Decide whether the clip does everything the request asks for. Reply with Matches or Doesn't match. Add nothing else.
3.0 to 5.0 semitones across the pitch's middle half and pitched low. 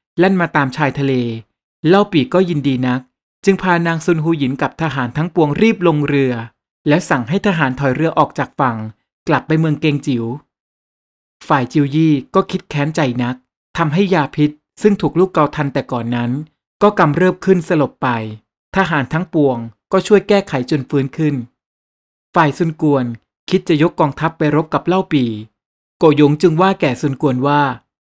Doesn't match